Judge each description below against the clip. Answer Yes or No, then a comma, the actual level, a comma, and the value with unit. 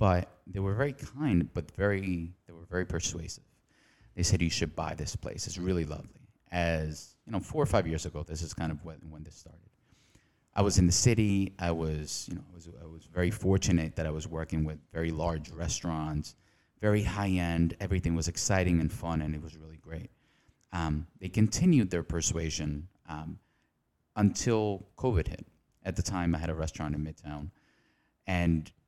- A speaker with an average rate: Yes, average, 190 wpm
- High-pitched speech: No, very low, 85 Hz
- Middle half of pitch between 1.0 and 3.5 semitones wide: Yes, average, 3.2 semitones